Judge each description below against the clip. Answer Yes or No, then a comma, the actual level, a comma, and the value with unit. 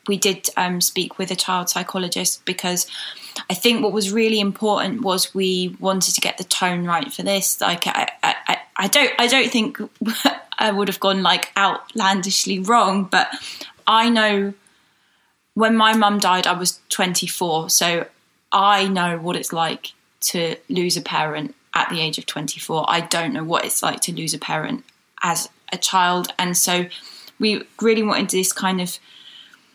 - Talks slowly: No, average, 175 wpm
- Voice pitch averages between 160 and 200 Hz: Yes, high, 190 Hz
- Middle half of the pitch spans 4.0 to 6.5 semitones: No, average, 3.0 semitones